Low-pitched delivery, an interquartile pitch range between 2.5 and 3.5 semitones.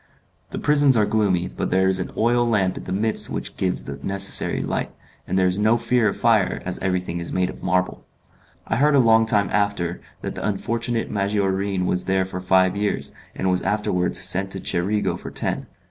Yes: low, 100 Hz; average, 2.9 semitones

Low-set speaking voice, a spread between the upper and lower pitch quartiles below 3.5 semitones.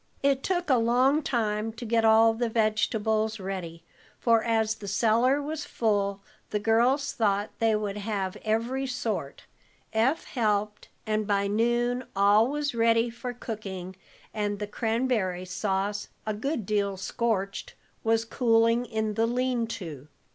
No: high, 225 Hz; narrow, 2.5 semitones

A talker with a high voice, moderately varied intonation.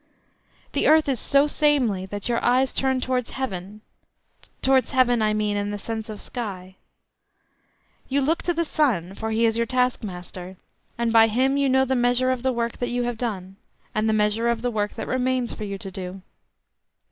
Yes: high, 235 Hz; average, 3.7 semitones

